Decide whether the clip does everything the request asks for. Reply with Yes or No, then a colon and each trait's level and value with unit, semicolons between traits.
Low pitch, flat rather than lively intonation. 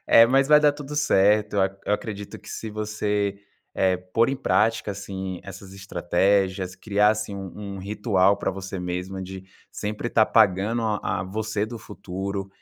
Yes: low, 100 Hz; narrow, 2.1 semitones